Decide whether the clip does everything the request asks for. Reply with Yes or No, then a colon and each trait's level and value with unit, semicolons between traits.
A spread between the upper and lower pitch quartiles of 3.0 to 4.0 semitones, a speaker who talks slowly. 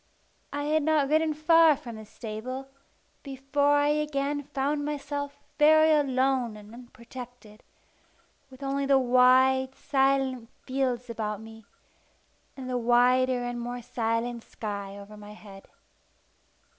Yes: average, 3.4 semitones; slow, 130 wpm